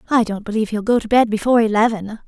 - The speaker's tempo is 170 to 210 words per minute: No, fast, 235 wpm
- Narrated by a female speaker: Yes, female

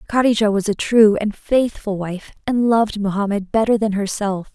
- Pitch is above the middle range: Yes, high, 210 Hz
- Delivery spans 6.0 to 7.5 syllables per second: No, 5.0 syllables/s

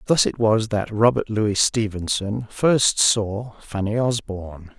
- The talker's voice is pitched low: Yes, low, 110 Hz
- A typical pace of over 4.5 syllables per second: No, 3.8 syllables/s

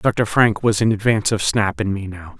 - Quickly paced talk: Yes, fast, 250 wpm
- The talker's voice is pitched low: Yes, low, 105 Hz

